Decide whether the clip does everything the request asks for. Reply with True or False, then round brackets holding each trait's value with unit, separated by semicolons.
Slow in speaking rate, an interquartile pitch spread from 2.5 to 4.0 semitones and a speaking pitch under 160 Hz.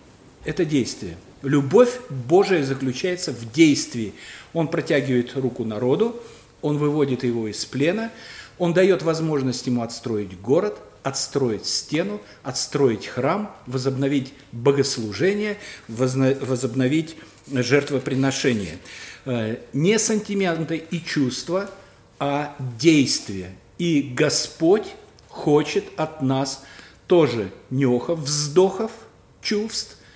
False (90 wpm; 4.8 semitones; 140 Hz)